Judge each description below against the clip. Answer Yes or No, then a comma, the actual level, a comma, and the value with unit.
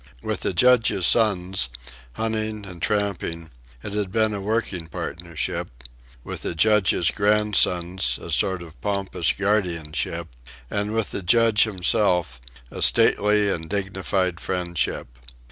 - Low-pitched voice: Yes, very low, 95 Hz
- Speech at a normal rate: No, slow, 125 wpm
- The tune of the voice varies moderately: Yes, average, 3.4 semitones